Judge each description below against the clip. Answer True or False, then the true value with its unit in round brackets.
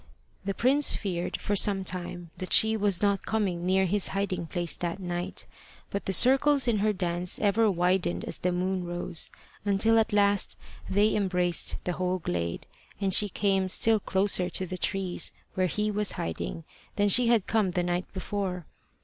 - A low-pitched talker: False (190 Hz)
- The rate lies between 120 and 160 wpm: False (175 wpm)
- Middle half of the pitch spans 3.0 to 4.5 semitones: False (2.6 semitones)